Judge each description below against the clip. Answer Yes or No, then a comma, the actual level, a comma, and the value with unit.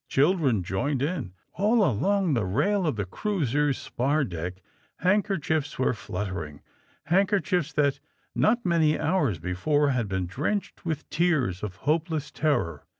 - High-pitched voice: No, medium, 145 Hz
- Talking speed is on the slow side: No, average, 150 wpm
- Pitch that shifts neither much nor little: No, wide, 8.8 semitones